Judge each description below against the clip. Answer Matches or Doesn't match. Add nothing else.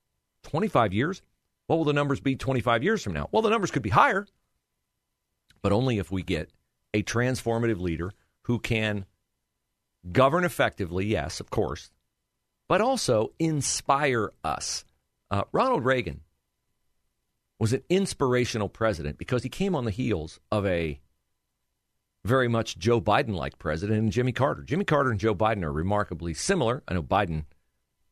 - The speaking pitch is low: Matches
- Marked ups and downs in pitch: Matches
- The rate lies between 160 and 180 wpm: Doesn't match